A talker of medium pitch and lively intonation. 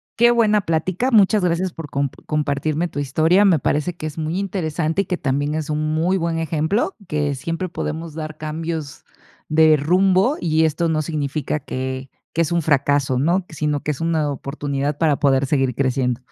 No: medium, 155 Hz; average, 3.0 semitones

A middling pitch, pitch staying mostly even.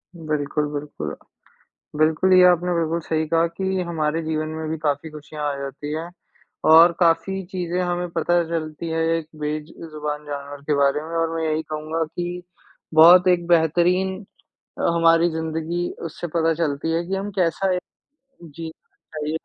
Yes: medium, 160 Hz; narrow, 2.1 semitones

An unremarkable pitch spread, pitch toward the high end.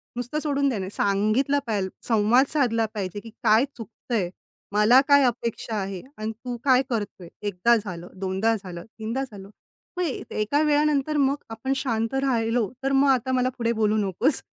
Yes: average, 4.4 semitones; high, 230 Hz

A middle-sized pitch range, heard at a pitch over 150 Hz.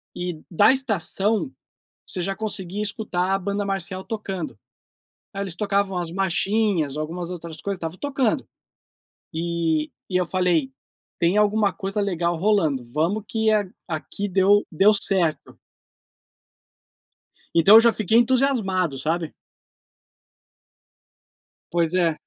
Yes: average, 3.6 semitones; high, 190 Hz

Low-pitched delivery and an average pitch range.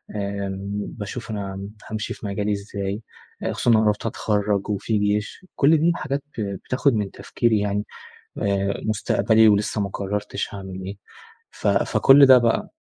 No: low, 105 Hz; narrow, 2.0 semitones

